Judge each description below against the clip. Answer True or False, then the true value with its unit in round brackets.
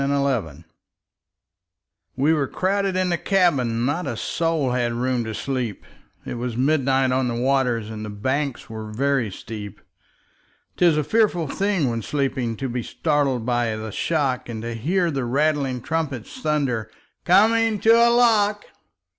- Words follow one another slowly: False (155 wpm)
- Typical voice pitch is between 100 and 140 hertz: True (135 Hz)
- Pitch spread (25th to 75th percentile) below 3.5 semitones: False (5.5 semitones)